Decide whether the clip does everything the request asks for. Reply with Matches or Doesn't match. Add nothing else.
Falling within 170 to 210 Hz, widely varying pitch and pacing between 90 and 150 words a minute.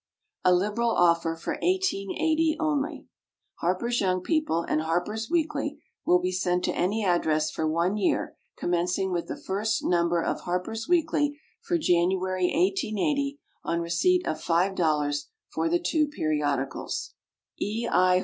Matches